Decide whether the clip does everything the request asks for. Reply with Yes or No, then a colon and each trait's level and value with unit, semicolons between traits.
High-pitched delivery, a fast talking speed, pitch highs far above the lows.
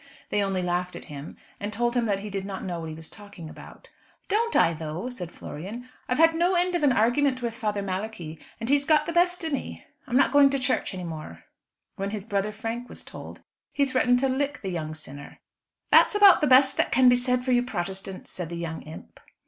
Yes: high, 225 Hz; fast, 230 wpm; wide, 6.6 semitones